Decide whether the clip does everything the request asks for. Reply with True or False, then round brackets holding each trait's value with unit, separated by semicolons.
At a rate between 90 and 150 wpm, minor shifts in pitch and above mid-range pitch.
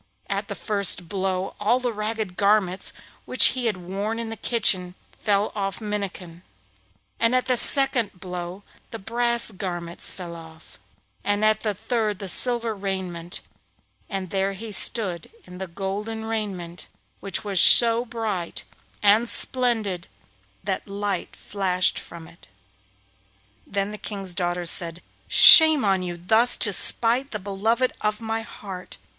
False (145 wpm; 3.5 semitones; 200 Hz)